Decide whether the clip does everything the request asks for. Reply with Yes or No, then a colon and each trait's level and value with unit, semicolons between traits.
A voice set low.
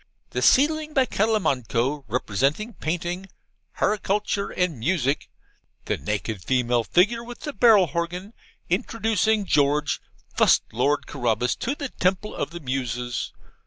No: medium, 170 Hz